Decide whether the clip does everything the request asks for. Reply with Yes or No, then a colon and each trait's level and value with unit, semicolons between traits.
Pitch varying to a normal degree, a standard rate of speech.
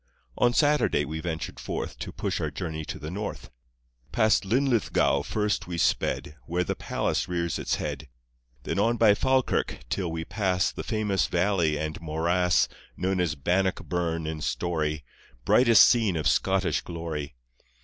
Yes: average, 4.4 semitones; average, 150 wpm